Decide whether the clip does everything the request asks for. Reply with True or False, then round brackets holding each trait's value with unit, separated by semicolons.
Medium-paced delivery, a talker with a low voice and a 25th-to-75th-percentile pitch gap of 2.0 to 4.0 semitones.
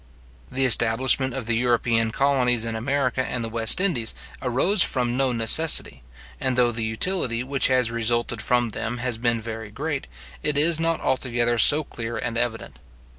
True (170 wpm; 120 Hz; 2.5 semitones)